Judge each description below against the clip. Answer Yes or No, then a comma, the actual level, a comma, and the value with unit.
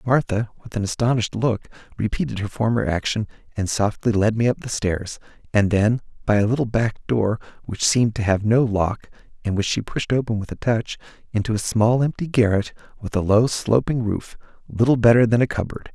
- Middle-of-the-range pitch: No, low, 110 Hz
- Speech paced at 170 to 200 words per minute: Yes, average, 195 wpm